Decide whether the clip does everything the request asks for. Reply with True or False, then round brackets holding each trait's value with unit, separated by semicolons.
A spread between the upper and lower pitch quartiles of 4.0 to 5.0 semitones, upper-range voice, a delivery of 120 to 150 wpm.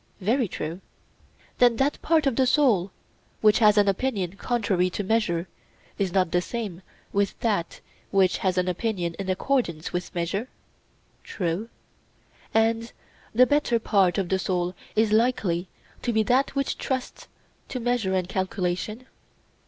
True (4.5 semitones; 205 Hz; 145 wpm)